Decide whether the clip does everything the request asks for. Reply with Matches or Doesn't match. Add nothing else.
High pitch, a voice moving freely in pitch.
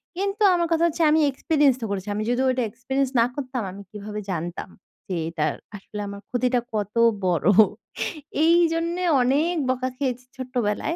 Matches